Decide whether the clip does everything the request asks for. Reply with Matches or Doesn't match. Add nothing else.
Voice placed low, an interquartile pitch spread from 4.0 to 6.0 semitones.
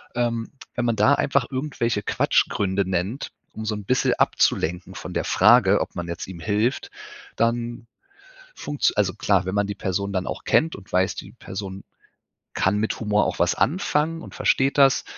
Matches